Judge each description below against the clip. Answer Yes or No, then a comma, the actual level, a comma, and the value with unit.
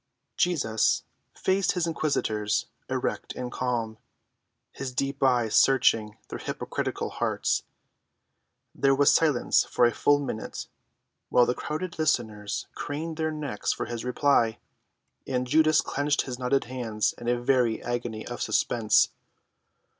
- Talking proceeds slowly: Yes, slow, 130 wpm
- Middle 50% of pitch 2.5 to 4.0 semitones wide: Yes, average, 3.7 semitones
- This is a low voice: Yes, low, 125 Hz